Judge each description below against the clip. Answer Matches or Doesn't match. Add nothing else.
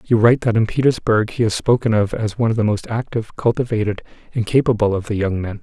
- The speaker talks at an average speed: Doesn't match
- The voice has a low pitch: Matches